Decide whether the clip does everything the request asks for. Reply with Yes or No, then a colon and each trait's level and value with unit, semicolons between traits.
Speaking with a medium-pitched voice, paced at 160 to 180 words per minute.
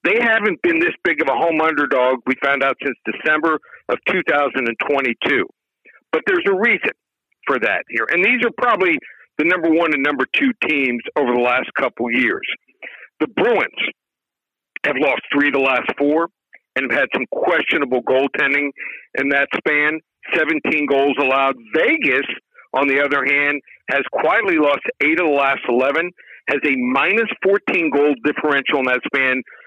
Yes: medium, 145 Hz; average, 165 wpm